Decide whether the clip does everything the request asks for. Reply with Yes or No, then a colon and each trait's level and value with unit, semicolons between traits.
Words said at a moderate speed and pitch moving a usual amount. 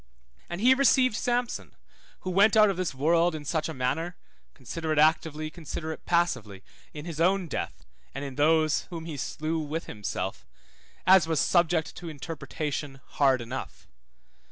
Yes: average, 160 wpm; average, 3.2 semitones